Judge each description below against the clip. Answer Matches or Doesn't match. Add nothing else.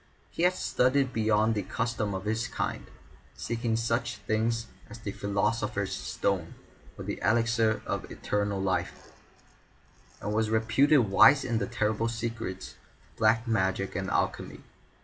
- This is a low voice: Matches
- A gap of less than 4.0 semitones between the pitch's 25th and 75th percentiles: Matches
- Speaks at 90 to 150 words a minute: Matches